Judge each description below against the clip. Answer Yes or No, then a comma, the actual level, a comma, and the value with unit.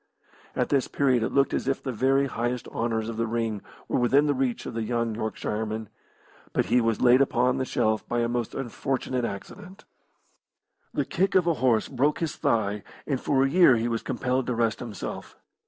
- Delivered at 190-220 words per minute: Yes, average, 200 wpm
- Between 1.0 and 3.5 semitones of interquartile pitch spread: Yes, average, 2.9 semitones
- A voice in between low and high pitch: No, low, 120 Hz